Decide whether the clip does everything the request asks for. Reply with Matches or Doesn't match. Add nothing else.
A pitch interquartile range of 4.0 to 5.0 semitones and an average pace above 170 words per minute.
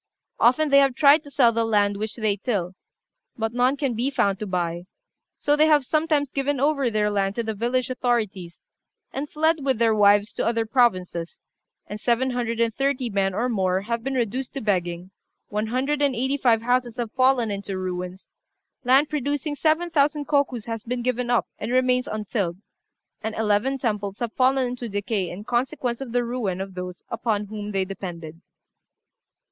Matches